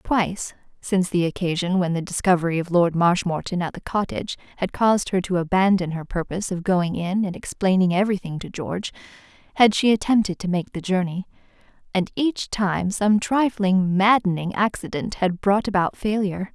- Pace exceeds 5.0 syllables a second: Yes, 5.5 syllables/s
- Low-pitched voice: No, high, 190 Hz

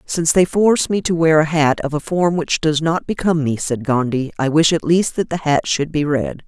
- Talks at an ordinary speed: No, fast, 260 wpm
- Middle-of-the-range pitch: Yes, medium, 160 Hz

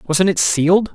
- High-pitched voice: No, medium, 180 Hz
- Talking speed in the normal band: Yes, average, 190 wpm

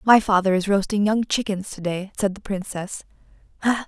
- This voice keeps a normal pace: Yes, average, 170 wpm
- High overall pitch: Yes, high, 200 Hz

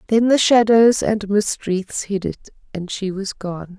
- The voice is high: Yes, high, 205 Hz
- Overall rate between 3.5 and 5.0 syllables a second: Yes, 3.9 syllables/s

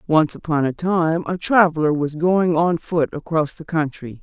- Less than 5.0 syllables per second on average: Yes, 4.5 syllables/s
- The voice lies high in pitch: No, medium, 160 Hz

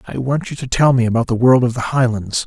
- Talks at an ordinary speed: No, fast, 290 wpm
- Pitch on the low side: Yes, low, 125 Hz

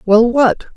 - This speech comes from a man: Yes, male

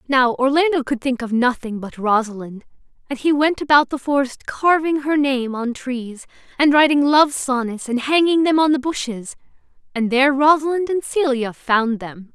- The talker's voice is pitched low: No, very high, 270 Hz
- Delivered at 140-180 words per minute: Yes, average, 175 wpm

